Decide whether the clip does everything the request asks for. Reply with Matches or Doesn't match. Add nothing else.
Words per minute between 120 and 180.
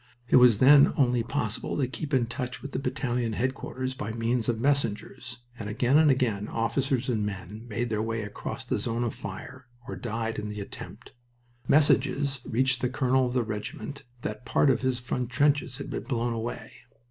Doesn't match